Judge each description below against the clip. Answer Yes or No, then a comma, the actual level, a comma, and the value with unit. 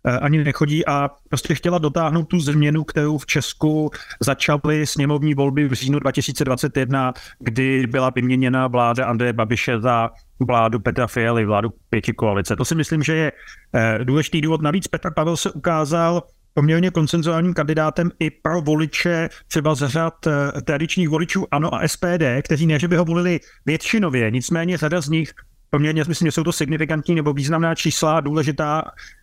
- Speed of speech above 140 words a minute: Yes, average, 160 wpm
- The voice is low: No, medium, 155 Hz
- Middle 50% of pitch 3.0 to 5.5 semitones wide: Yes, average, 3.7 semitones